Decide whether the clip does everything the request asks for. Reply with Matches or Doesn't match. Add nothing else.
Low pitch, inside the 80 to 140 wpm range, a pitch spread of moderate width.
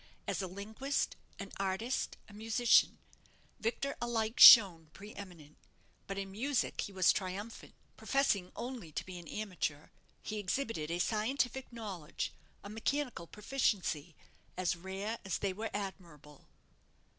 Doesn't match